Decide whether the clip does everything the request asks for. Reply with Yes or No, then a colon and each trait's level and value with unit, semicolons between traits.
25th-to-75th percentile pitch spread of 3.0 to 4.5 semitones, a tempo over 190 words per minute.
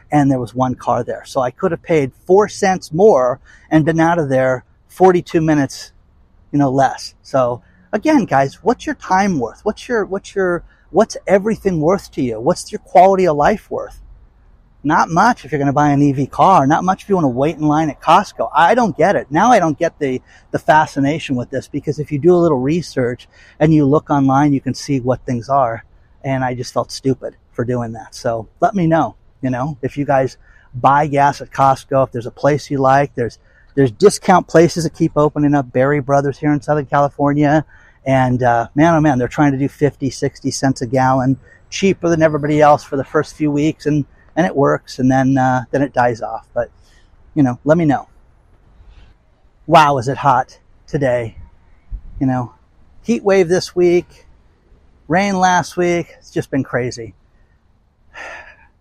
Yes: average, 4.2 semitones; average, 200 wpm